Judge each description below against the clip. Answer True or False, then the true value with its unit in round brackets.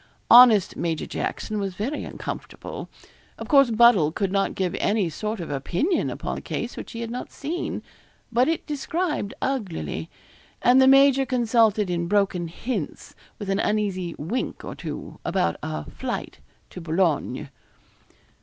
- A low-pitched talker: False (210 Hz)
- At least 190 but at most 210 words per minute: False (150 wpm)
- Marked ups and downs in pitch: True (6.3 semitones)